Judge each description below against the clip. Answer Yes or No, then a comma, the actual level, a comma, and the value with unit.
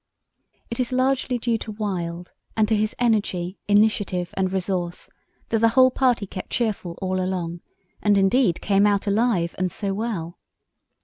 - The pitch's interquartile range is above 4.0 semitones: No, average, 3.7 semitones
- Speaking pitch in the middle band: No, high, 205 Hz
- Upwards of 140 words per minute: Yes, average, 160 wpm